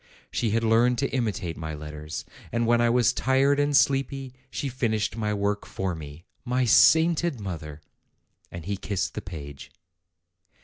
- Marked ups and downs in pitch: Yes, wide, 6.8 semitones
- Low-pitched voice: Yes, low, 115 Hz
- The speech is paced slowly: No, average, 160 wpm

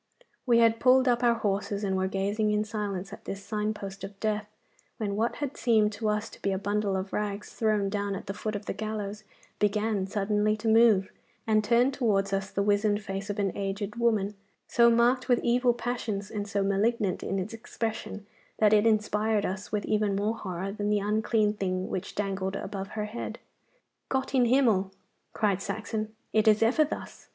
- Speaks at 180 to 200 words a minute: Yes, average, 195 wpm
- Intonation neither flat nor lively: No, narrow, 2.0 semitones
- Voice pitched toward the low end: No, high, 210 Hz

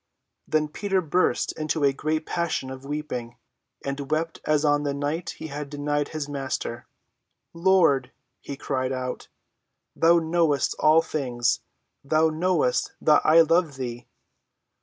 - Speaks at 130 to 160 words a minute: Yes, average, 140 wpm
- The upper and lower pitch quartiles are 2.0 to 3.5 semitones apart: Yes, average, 2.9 semitones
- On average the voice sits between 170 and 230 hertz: No, medium, 150 Hz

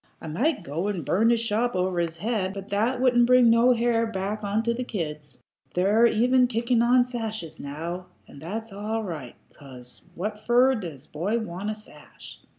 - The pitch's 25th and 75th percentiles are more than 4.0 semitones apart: Yes, average, 5.1 semitones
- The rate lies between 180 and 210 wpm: Yes, average, 185 wpm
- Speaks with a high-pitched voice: Yes, high, 215 Hz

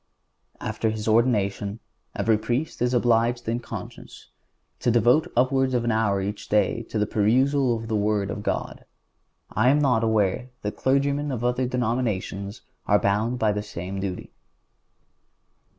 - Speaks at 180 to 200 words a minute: No, average, 155 wpm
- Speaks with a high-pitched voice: No, low, 115 Hz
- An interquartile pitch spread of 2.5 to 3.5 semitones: Yes, average, 3.1 semitones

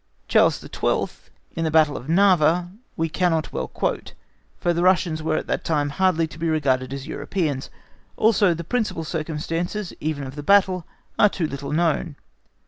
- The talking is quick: No, average, 170 wpm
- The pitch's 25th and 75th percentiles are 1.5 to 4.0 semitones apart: Yes, average, 3.1 semitones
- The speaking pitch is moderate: Yes, medium, 160 Hz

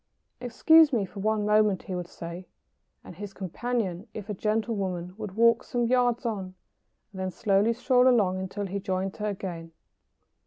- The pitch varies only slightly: No, average, 3.7 semitones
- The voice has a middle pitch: No, high, 205 Hz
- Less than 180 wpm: Yes, average, 170 wpm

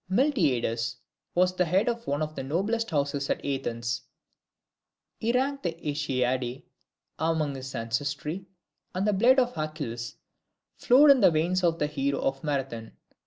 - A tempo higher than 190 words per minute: No, average, 150 wpm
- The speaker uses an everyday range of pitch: No, wide, 5.9 semitones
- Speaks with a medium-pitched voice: Yes, medium, 155 Hz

